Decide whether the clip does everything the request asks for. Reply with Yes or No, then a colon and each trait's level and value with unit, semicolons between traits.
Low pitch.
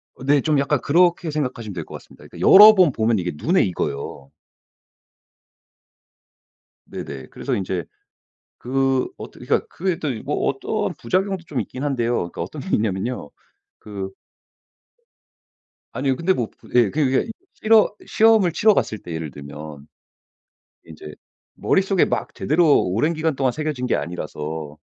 Yes: low, 130 Hz